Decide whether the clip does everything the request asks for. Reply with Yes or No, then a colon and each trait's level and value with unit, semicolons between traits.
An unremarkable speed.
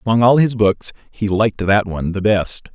No: fast, 220 wpm